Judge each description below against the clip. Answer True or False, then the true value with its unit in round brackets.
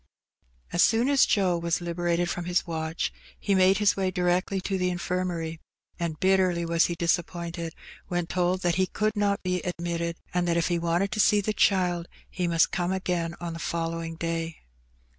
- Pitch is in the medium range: True (175 Hz)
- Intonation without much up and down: True (1.7 semitones)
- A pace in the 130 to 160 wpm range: False (190 wpm)